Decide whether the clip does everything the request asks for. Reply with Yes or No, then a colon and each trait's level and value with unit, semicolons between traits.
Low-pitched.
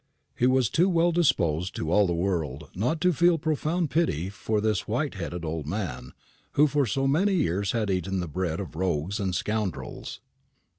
Yes: low, 100 Hz